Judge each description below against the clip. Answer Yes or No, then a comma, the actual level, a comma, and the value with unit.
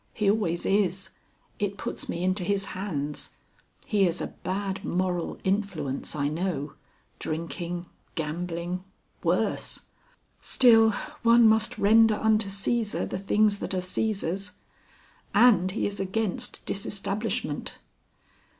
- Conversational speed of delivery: No, slow, 115 wpm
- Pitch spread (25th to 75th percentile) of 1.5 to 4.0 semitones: Yes, average, 3.1 semitones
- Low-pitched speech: No, high, 195 Hz